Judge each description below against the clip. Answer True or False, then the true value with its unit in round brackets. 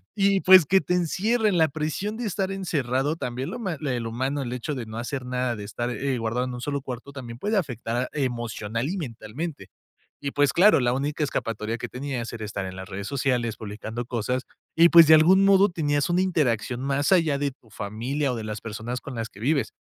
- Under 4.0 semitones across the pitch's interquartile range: False (5.3 semitones)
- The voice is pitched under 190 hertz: True (135 Hz)